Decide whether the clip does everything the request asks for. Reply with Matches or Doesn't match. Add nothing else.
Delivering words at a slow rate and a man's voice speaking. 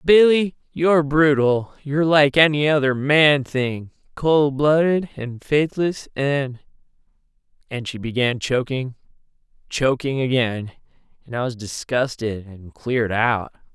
Matches